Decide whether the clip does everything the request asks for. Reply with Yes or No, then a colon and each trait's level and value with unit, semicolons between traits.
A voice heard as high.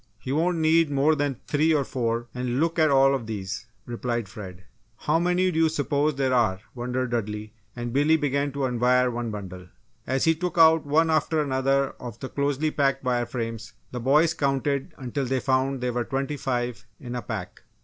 No: low, 135 Hz